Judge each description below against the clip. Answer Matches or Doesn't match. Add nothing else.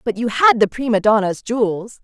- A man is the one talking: Doesn't match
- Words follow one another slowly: Doesn't match